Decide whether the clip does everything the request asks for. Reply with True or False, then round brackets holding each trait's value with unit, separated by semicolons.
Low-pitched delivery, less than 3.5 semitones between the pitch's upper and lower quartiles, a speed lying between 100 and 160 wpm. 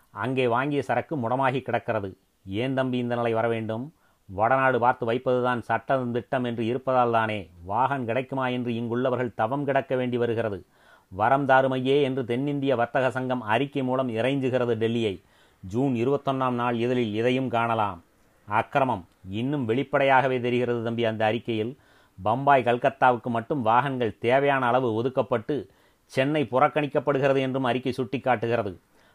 True (125 Hz; 2.4 semitones; 120 wpm)